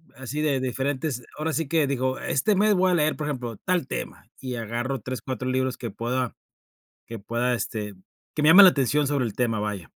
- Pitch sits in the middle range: No, low, 130 Hz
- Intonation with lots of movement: No, average, 4.0 semitones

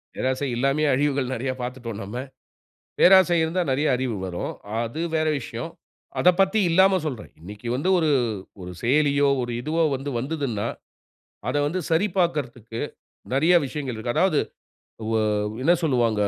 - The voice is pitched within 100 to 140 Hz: Yes, low, 135 Hz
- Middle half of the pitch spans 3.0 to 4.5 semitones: No, average, 5.1 semitones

